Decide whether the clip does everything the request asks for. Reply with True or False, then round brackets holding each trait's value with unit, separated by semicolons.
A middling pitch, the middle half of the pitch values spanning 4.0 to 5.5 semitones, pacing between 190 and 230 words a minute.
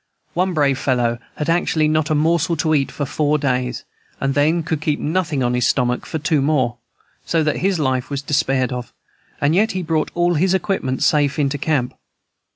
False (150 Hz; 3.4 semitones; 200 wpm)